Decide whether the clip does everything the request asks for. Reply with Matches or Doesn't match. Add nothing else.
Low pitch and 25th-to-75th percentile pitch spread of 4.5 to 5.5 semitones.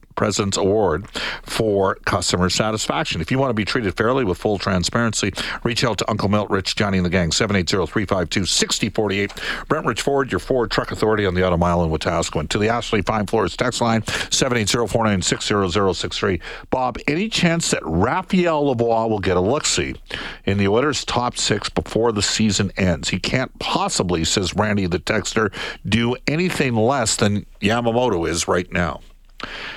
Doesn't match